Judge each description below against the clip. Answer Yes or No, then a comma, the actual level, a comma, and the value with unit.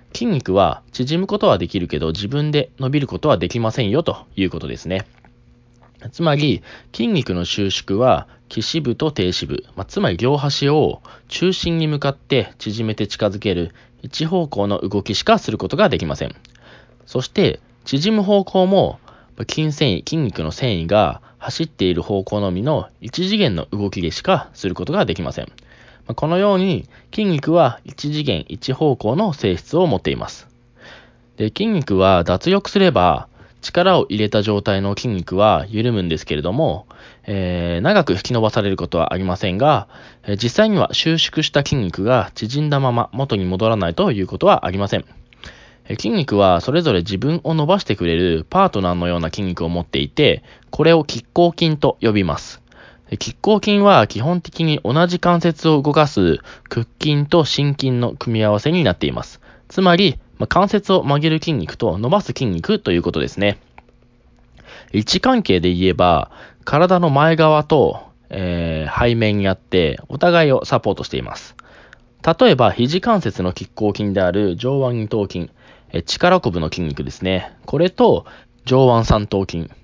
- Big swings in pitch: Yes, wide, 8.7 semitones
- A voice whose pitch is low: Yes, low, 120 Hz